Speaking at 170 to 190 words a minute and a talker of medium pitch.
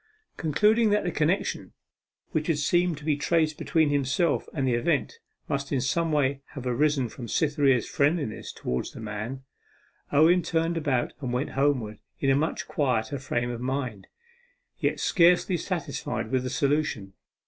No: average, 160 wpm; medium, 145 Hz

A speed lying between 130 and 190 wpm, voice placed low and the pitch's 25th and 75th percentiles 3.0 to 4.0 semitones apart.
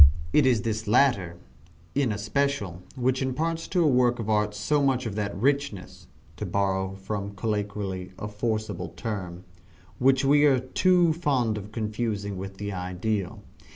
No: average, 155 wpm; low, 110 Hz; average, 4.8 semitones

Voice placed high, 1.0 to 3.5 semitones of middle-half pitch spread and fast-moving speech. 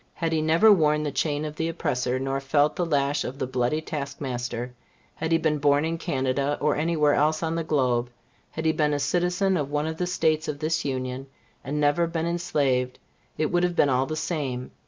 No: medium, 150 Hz; average, 2.9 semitones; fast, 220 wpm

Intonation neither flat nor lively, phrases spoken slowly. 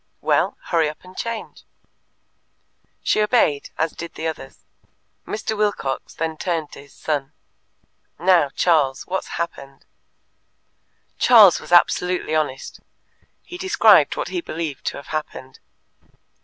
Yes: average, 4.4 semitones; slow, 125 wpm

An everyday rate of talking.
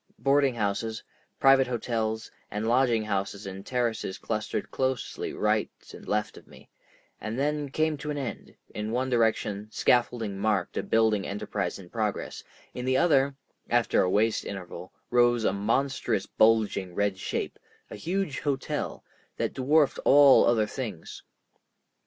Yes: average, 145 wpm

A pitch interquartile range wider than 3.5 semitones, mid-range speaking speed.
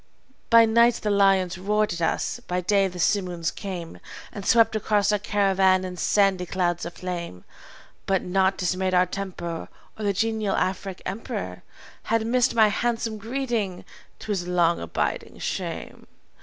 No: average, 2.9 semitones; average, 155 wpm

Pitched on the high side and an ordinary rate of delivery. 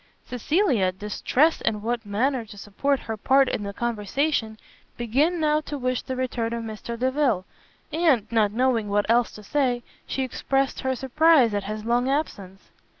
Yes: high, 240 Hz; average, 165 wpm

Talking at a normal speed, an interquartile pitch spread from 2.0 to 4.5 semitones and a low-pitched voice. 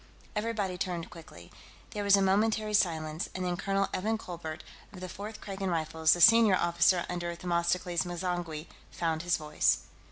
No: average, 160 wpm; narrow, 2.5 semitones; medium, 180 Hz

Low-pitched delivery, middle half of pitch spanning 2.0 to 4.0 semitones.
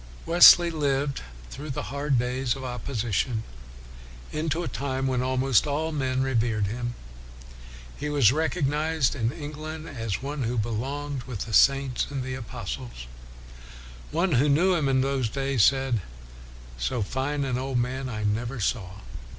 Yes: low, 130 Hz; average, 3.4 semitones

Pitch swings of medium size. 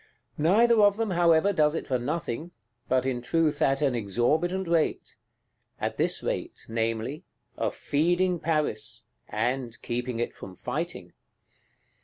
No: wide, 6.0 semitones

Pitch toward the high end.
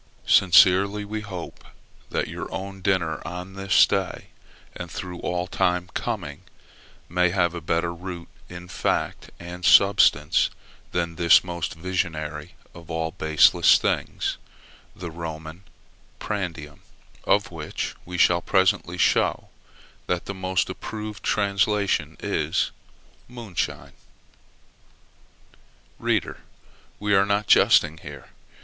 No: very low, 90 Hz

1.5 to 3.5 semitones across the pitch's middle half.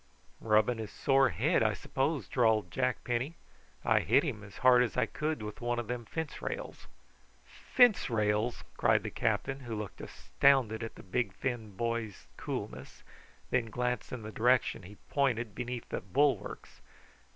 Yes: average, 3.0 semitones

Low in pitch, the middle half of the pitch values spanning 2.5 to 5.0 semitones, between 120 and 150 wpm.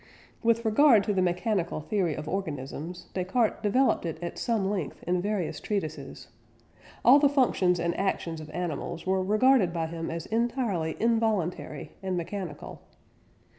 No: medium, 185 Hz; average, 4.6 semitones; average, 145 wpm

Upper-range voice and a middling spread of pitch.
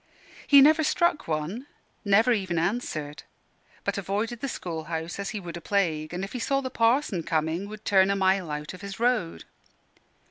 No: high, 195 Hz; wide, 5.7 semitones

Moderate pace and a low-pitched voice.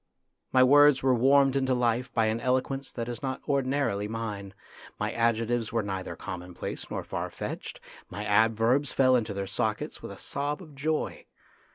Yes: average, 175 wpm; low, 120 Hz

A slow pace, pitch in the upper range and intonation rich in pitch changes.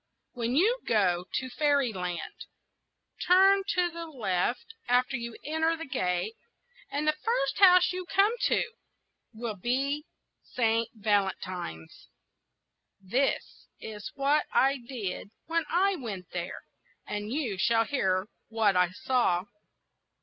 Yes: slow, 125 wpm; high, 245 Hz; wide, 7.8 semitones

